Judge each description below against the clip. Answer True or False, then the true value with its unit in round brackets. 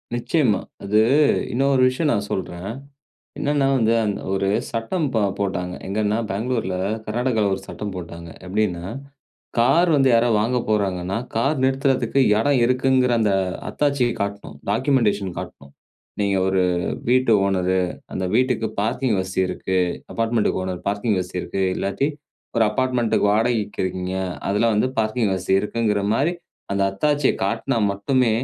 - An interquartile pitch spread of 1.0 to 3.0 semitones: False (4.5 semitones)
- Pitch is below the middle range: True (110 Hz)